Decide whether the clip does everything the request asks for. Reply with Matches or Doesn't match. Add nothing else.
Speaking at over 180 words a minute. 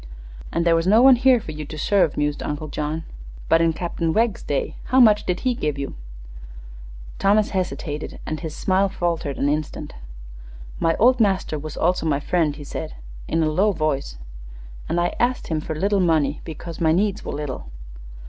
Matches